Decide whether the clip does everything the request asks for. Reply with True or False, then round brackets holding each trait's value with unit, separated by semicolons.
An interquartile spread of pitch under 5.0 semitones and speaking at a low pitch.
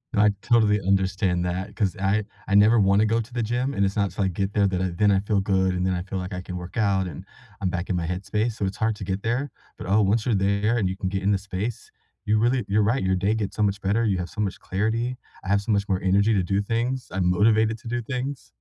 True (2.7 semitones; 100 Hz)